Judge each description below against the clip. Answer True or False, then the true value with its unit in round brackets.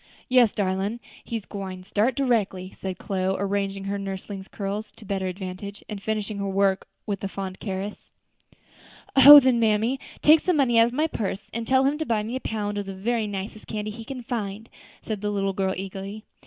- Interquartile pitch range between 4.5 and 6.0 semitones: False (2.9 semitones)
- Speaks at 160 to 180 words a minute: False (195 wpm)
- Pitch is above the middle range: True (205 Hz)